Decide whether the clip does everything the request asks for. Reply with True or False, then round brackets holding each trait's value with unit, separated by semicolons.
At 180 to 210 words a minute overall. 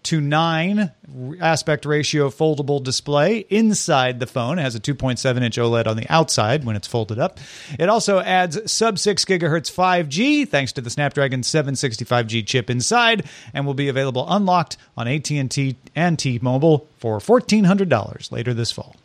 False (160 wpm)